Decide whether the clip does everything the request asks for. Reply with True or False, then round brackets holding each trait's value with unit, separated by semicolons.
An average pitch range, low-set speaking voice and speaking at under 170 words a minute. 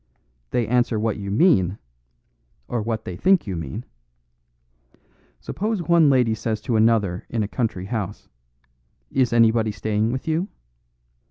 True (3.2 semitones; 110 Hz; 140 wpm)